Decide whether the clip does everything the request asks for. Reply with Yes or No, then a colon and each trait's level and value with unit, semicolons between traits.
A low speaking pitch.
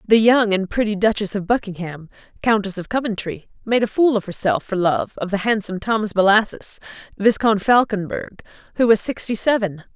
No: high, 210 Hz